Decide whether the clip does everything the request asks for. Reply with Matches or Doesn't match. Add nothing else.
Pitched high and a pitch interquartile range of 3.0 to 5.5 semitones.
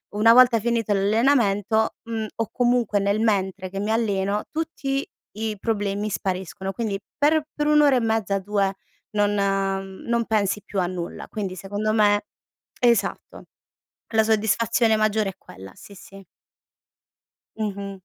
Doesn't match